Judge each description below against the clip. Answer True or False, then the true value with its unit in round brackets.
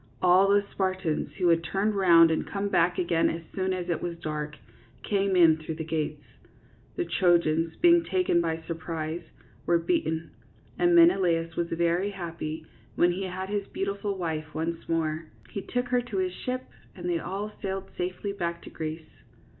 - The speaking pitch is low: False (175 Hz)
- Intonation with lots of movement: False (3.1 semitones)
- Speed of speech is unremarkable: True (175 wpm)